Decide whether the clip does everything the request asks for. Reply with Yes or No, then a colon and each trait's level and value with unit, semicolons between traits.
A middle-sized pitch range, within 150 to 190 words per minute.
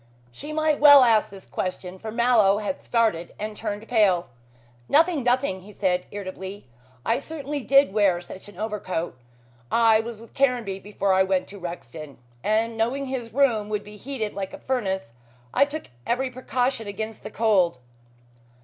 Yes: average, 4.6 semitones; average, 160 wpm